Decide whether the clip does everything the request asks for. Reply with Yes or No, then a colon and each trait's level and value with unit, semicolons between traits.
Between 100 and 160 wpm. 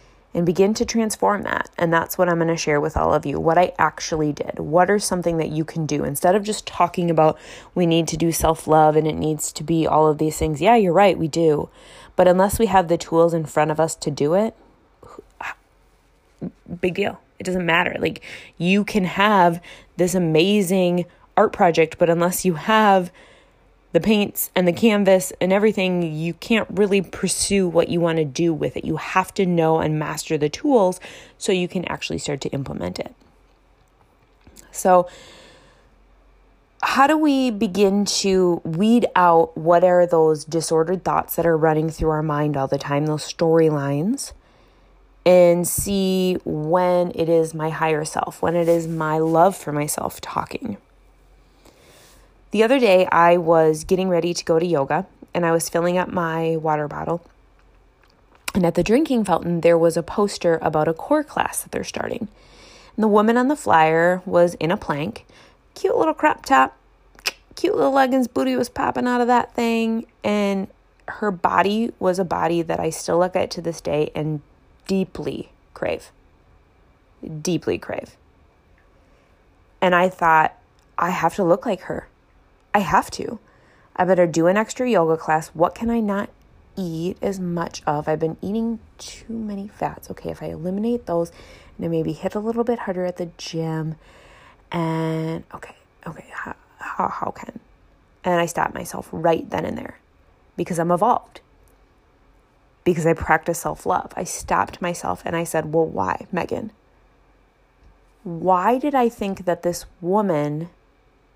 No: average, 170 wpm